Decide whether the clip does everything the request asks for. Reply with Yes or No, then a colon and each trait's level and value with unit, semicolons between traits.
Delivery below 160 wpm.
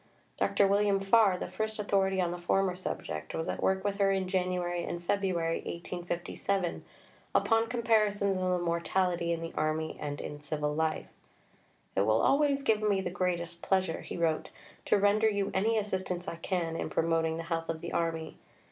No: average, 180 wpm